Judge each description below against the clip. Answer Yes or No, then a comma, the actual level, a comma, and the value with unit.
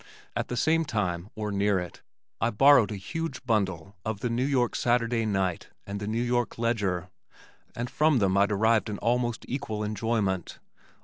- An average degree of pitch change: Yes, average, 3.3 semitones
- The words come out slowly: No, average, 175 wpm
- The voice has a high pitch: No, low, 110 Hz